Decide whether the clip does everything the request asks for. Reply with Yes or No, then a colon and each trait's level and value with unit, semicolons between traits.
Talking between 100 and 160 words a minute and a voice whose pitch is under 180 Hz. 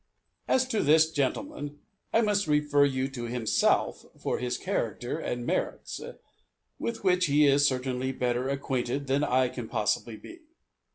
Yes: average, 150 wpm; medium, 140 Hz